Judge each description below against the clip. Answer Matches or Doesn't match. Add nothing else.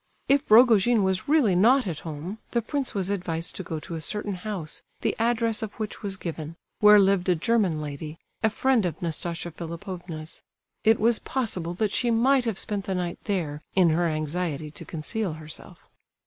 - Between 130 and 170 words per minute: Doesn't match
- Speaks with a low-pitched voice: Doesn't match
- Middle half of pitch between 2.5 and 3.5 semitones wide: Doesn't match